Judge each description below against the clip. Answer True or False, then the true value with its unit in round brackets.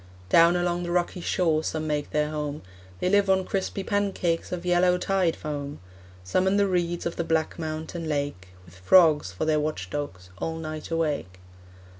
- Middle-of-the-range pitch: True (160 Hz)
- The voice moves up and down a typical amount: True (3.1 semitones)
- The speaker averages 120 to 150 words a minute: False (180 wpm)